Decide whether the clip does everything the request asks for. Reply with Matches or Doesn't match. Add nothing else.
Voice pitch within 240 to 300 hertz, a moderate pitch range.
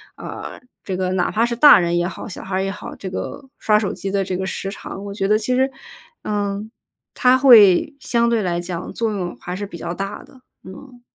Doesn't match